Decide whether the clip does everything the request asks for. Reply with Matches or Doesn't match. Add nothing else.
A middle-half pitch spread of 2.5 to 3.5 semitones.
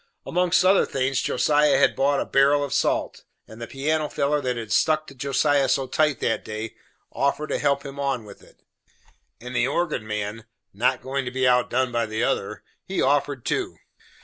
Matches